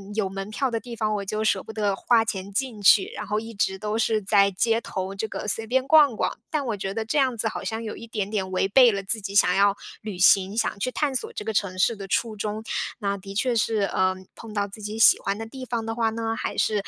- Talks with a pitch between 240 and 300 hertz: No, high, 215 Hz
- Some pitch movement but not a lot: No, narrow, 2.3 semitones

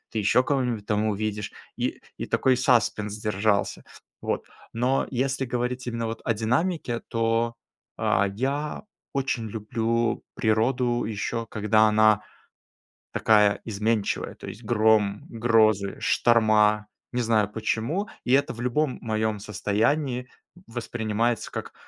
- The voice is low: Yes, low, 115 Hz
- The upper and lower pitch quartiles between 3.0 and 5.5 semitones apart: No, narrow, 2.4 semitones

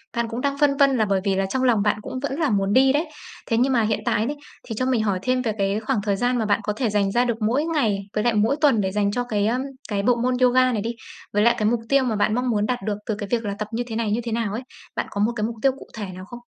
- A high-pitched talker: Yes, high, 230 Hz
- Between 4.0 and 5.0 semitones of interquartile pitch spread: No, average, 3.4 semitones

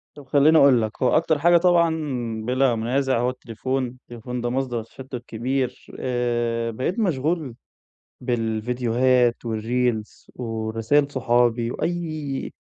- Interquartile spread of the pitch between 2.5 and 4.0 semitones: Yes, average, 2.8 semitones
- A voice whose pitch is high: No, low, 125 Hz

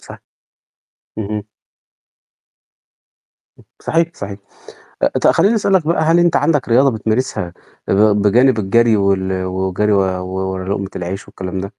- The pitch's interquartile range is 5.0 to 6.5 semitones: Yes, wide, 5.6 semitones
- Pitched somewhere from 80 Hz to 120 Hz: Yes, low, 105 Hz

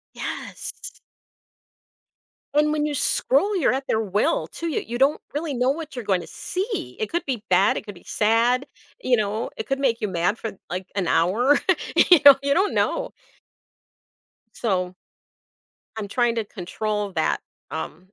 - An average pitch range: No, wide, 6.2 semitones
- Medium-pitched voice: No, high, 240 Hz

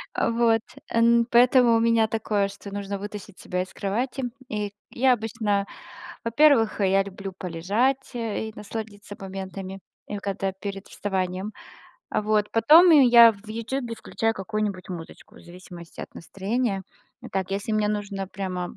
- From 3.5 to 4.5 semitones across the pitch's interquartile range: No, average, 2.9 semitones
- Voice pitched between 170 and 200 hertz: No, high, 210 Hz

